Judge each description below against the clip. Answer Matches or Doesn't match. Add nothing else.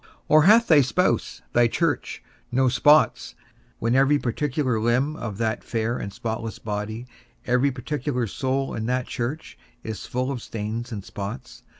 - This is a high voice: Doesn't match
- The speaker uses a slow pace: Doesn't match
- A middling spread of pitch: Matches